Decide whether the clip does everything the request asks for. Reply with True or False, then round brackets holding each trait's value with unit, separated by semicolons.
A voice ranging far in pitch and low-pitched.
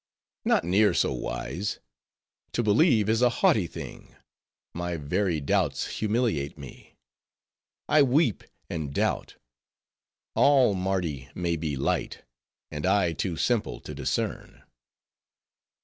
True (6.0 semitones; 90 Hz)